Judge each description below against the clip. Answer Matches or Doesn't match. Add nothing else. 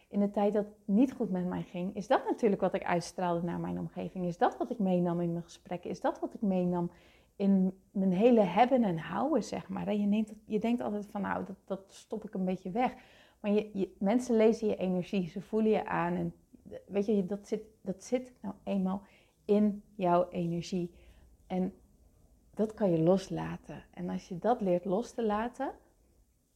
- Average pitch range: Matches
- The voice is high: Matches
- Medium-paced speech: Doesn't match